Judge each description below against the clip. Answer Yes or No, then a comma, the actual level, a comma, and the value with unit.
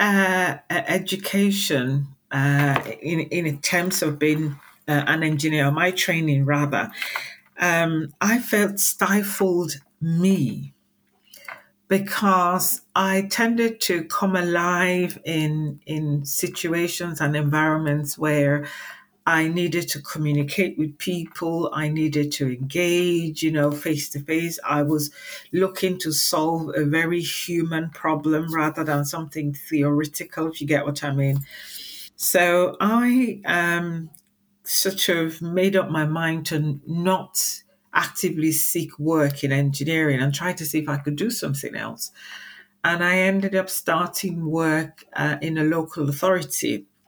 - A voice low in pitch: No, medium, 160 Hz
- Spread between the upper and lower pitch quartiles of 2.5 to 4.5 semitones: Yes, average, 3.4 semitones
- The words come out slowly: Yes, slow, 130 wpm